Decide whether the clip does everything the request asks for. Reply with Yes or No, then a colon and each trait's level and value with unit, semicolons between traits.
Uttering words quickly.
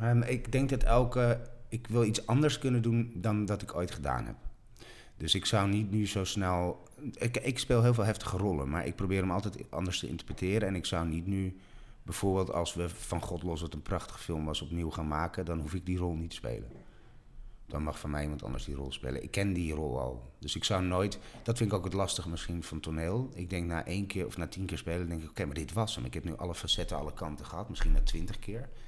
Yes: fast, 255 wpm